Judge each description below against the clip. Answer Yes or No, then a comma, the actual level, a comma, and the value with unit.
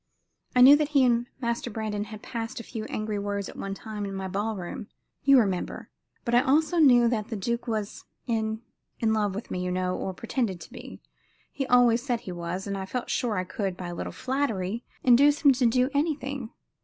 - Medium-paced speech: No, fast, 215 wpm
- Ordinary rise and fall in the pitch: Yes, average, 4.0 semitones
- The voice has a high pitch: Yes, high, 225 Hz